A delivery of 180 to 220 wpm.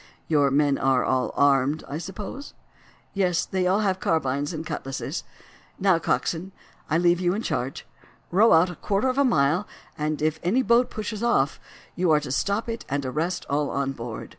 Yes: average, 185 wpm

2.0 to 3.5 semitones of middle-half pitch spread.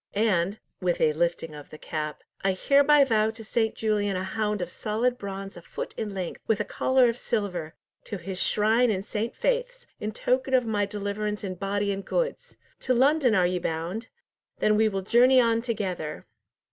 No: average, 3.9 semitones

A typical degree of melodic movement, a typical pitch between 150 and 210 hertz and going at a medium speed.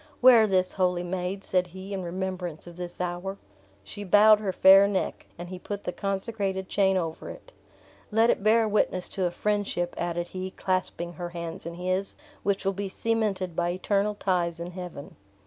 No: narrow, 2.3 semitones; medium, 185 Hz; average, 180 wpm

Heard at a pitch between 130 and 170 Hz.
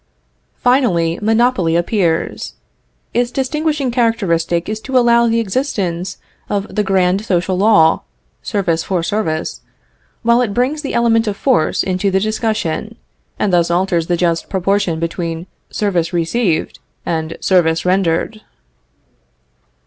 No: high, 195 Hz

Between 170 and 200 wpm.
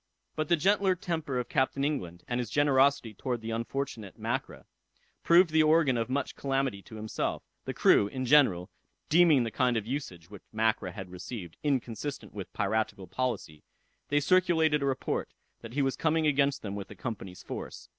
Yes: average, 175 wpm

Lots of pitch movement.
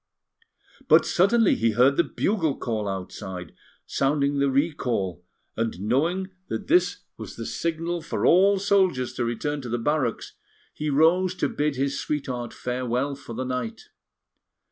Yes: wide, 5.7 semitones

